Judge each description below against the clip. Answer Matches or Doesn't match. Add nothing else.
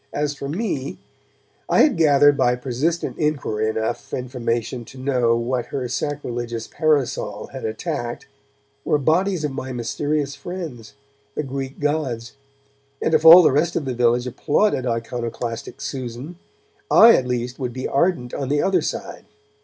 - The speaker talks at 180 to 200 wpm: Doesn't match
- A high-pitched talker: Doesn't match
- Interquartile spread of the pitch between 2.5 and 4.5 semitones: Matches